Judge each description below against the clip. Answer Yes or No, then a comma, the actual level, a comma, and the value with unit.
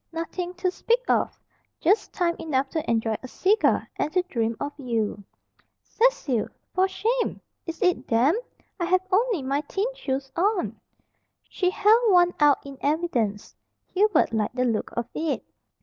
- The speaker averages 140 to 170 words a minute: Yes, average, 155 wpm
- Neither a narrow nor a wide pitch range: No, wide, 6.3 semitones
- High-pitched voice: Yes, very high, 330 Hz